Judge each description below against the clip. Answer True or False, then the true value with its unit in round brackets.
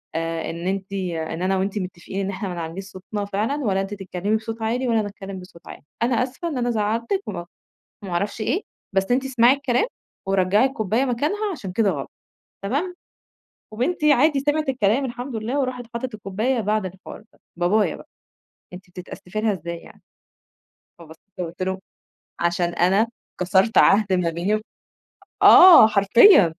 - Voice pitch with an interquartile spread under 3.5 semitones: False (4.8 semitones)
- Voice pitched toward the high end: True (205 Hz)